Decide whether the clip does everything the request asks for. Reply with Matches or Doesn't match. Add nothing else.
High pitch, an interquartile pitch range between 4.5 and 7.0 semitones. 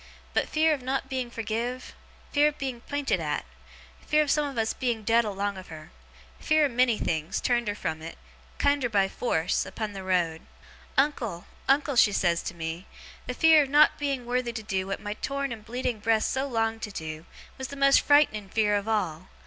Matches